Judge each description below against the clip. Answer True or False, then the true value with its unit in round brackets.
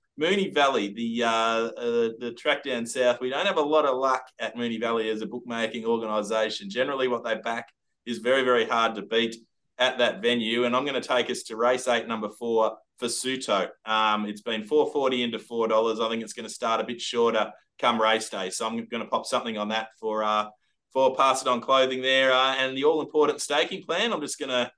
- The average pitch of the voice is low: True (115 Hz)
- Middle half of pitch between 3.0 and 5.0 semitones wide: False (2.5 semitones)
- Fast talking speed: True (225 wpm)